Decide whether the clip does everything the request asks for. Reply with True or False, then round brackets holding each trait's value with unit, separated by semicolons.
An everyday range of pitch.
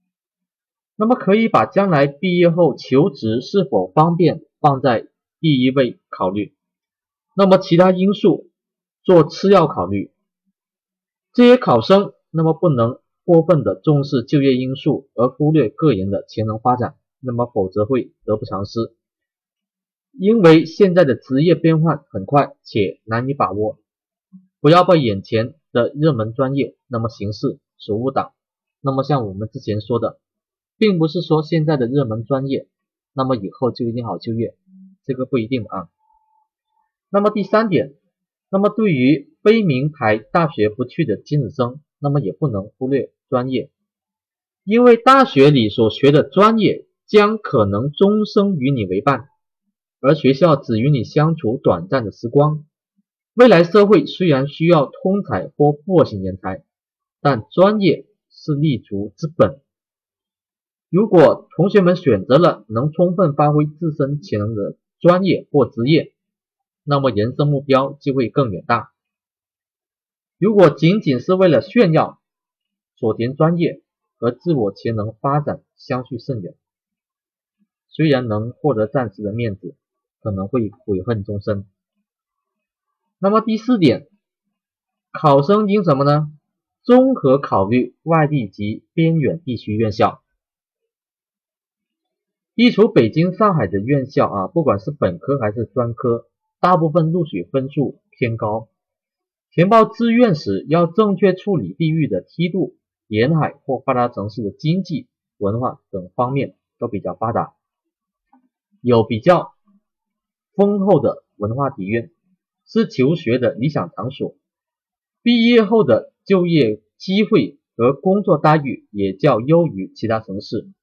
False (8.0 semitones)